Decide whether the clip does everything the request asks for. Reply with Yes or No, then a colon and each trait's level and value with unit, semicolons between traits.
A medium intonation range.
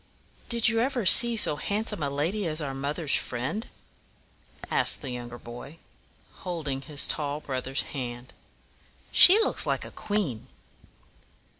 No: wide, 7.7 semitones